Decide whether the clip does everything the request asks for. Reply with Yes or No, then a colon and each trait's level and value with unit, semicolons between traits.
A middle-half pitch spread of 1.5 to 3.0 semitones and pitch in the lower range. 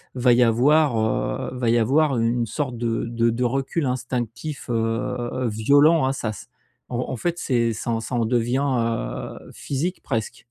Yes: average, 2.7 semitones; low, 120 Hz